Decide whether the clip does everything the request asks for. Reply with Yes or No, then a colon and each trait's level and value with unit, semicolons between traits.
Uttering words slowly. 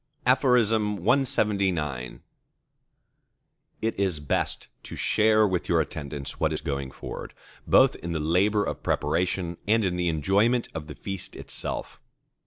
Yes: slow, 130 wpm